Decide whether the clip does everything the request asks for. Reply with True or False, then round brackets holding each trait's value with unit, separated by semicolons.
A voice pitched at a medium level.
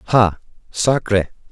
False (105 Hz)